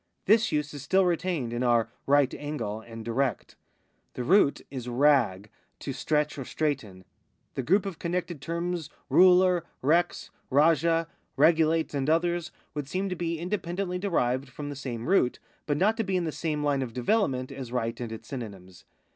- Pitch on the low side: No, medium, 150 Hz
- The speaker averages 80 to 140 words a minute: No, average, 170 wpm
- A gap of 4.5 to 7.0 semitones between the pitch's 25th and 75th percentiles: Yes, wide, 5.6 semitones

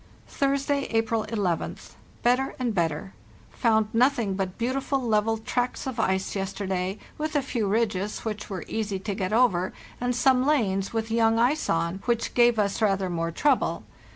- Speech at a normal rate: Yes, average, 160 wpm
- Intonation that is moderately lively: Yes, average, 4.1 semitones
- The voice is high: Yes, high, 220 Hz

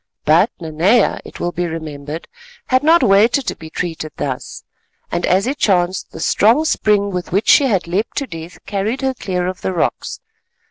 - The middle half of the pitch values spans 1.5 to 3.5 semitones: No, average, 5.3 semitones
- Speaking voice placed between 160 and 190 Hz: Yes, medium, 185 Hz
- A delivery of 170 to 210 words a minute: Yes, average, 185 wpm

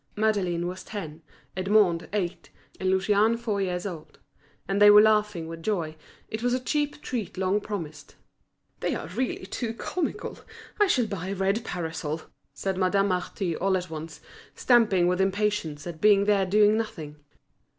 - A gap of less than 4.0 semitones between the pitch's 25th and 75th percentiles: Yes, average, 3.3 semitones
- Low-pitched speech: No, high, 195 Hz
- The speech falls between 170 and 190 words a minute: No, average, 160 wpm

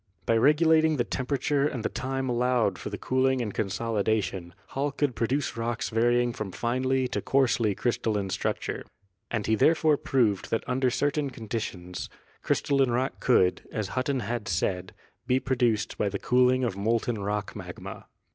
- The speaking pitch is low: Yes, low, 120 Hz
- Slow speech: No, average, 155 wpm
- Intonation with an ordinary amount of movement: Yes, average, 3.8 semitones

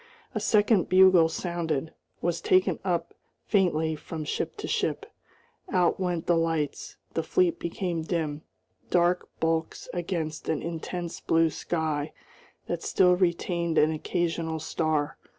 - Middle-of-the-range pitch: Yes, medium, 170 Hz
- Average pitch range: No, narrow, 2.0 semitones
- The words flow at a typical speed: No, slow, 130 wpm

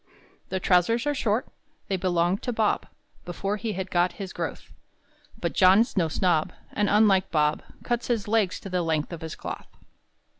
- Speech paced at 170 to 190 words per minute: Yes, average, 175 wpm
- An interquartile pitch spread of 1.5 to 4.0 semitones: Yes, average, 3.4 semitones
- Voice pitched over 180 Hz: Yes, high, 190 Hz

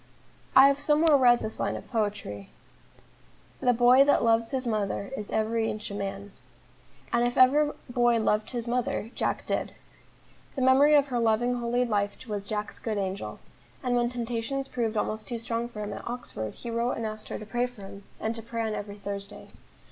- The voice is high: Yes, high, 230 Hz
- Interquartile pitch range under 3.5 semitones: Yes, average, 2.7 semitones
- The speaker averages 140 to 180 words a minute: No, average, 195 wpm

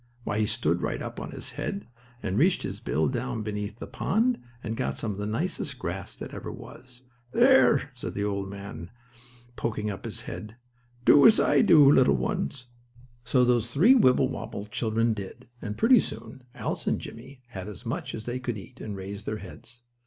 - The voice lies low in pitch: Yes, low, 115 Hz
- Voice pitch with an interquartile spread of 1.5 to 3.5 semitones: No, average, 4.4 semitones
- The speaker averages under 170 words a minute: No, average, 195 wpm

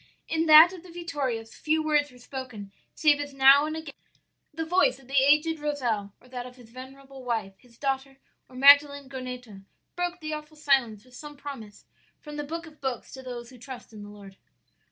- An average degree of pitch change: Yes, average, 3.4 semitones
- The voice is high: Yes, very high, 270 Hz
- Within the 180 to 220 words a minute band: Yes, average, 200 wpm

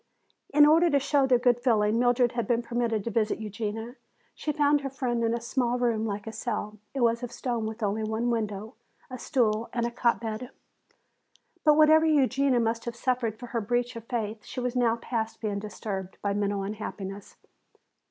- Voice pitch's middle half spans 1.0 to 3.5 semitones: Yes, narrow, 2.4 semitones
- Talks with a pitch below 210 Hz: No, high, 235 Hz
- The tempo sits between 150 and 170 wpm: No, average, 195 wpm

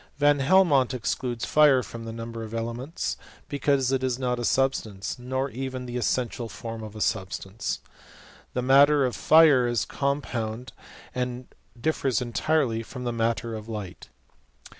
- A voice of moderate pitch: No, low, 125 Hz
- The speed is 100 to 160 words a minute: Yes, average, 150 wpm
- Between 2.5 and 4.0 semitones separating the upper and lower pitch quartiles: Yes, average, 2.8 semitones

